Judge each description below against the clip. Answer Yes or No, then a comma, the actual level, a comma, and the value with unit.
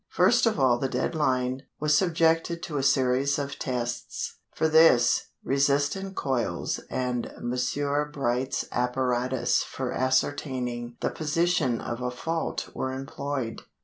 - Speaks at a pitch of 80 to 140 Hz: Yes, low, 135 Hz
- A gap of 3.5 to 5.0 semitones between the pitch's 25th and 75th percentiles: No, average, 3.1 semitones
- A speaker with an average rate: No, slow, 130 wpm